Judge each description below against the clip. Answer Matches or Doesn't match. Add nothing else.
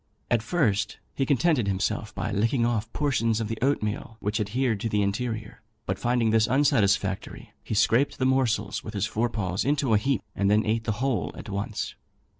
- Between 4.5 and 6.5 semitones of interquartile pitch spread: Doesn't match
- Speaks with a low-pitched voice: Matches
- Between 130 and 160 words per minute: Doesn't match